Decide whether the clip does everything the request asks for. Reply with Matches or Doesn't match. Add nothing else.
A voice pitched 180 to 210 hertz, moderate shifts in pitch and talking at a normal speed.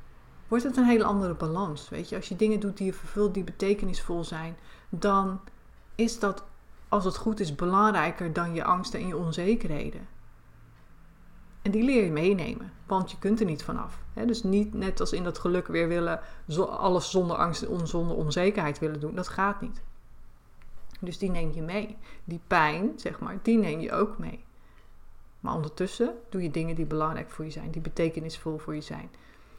Matches